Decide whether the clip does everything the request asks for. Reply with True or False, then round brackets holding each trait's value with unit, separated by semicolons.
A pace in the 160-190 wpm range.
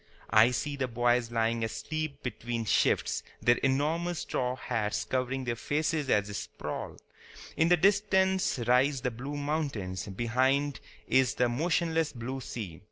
False (145 wpm)